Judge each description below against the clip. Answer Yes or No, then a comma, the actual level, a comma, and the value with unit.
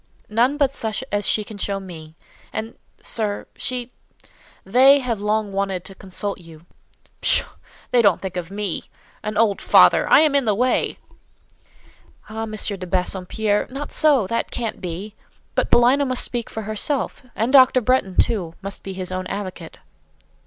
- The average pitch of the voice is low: No, high, 210 Hz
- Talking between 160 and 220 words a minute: No, average, 145 wpm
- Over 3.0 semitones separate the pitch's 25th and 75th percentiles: Yes, average, 4.2 semitones